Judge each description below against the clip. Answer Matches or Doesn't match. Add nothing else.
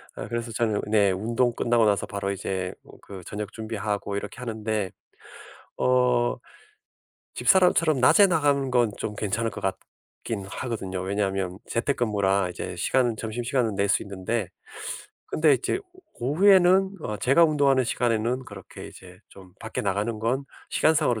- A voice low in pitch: Matches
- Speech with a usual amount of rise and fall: Matches